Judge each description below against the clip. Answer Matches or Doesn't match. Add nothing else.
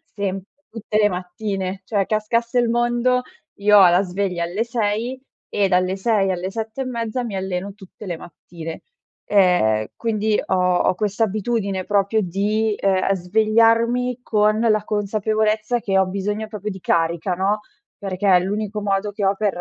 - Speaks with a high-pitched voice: Matches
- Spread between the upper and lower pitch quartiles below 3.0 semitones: Matches